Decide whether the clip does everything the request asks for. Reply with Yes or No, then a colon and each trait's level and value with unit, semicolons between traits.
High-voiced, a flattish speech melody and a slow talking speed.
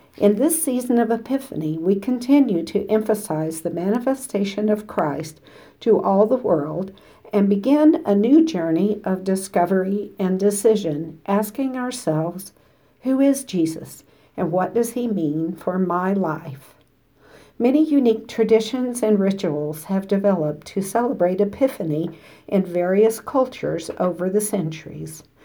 No: high, 200 Hz; wide, 5.5 semitones; slow, 130 wpm